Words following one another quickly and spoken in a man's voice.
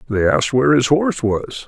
Yes: fast, 215 wpm; male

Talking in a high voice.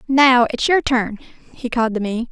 Yes: high, 240 Hz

